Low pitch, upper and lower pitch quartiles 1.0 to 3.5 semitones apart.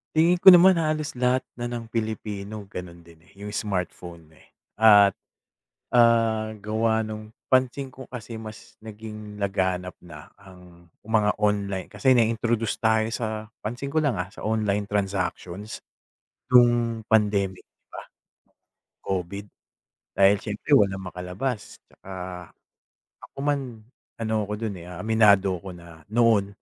Yes: low, 105 Hz; average, 2.9 semitones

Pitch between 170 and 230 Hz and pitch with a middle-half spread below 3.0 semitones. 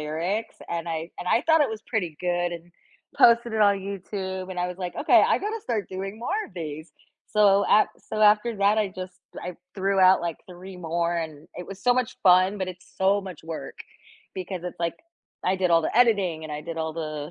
No: medium, 185 Hz; average, 3.6 semitones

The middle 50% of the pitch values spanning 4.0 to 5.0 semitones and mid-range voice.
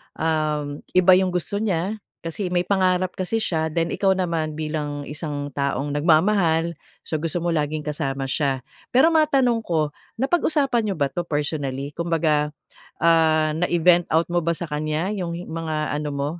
No: average, 3.2 semitones; medium, 165 Hz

